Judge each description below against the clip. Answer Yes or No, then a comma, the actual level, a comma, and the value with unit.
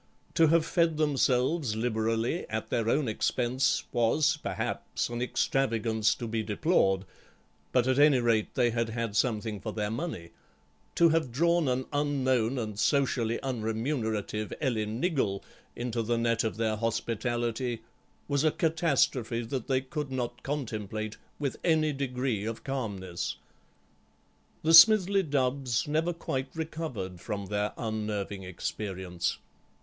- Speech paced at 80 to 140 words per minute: Yes, slow, 135 wpm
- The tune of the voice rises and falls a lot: No, average, 4.5 semitones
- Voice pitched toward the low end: Yes, low, 120 Hz